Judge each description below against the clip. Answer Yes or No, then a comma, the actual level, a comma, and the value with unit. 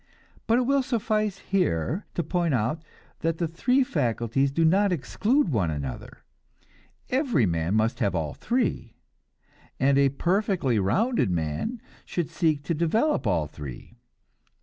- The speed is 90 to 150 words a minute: Yes, average, 140 wpm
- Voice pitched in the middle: Yes, medium, 160 Hz